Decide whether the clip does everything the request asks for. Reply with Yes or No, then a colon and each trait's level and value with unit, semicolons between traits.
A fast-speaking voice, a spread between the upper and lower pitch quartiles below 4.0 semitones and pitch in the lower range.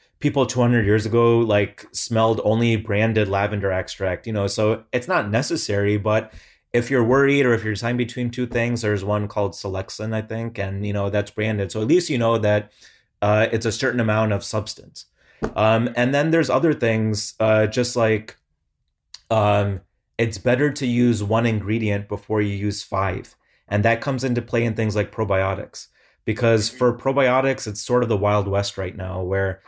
No: average, 185 wpm; narrow, 2.5 semitones; low, 110 Hz